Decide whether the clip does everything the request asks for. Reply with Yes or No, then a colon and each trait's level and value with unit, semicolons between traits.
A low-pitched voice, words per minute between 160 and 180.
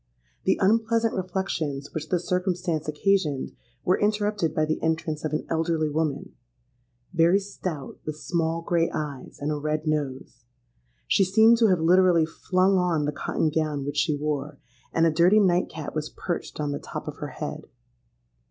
No: medium, 160 Hz; average, 165 wpm